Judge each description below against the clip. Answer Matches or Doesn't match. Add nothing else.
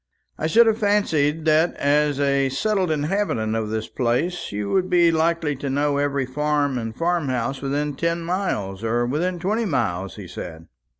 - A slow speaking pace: Doesn't match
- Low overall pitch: Doesn't match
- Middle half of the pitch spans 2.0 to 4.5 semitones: Doesn't match